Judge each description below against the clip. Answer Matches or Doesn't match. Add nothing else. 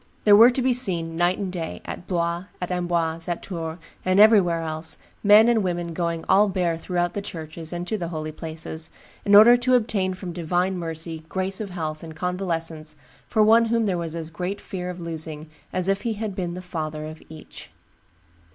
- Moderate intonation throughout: Matches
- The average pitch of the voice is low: Doesn't match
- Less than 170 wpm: Doesn't match